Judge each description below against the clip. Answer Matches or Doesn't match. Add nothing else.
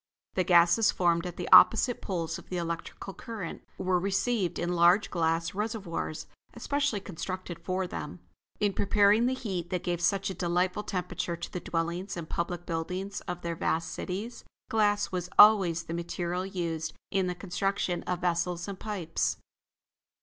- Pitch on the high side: Doesn't match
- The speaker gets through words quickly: Doesn't match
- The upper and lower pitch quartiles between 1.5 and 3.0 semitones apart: Matches